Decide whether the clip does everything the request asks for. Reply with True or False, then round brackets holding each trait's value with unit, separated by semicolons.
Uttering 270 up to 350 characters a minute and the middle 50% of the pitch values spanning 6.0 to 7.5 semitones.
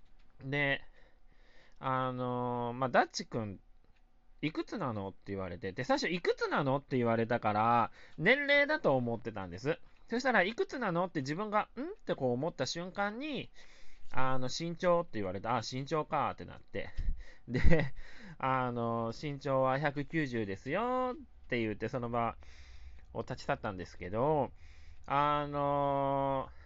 True (285 characters per minute; 6.8 semitones)